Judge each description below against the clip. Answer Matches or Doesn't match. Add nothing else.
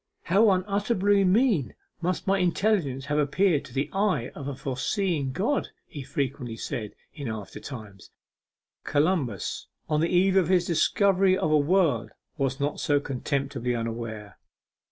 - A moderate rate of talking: Matches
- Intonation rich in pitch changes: Matches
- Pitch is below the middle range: Doesn't match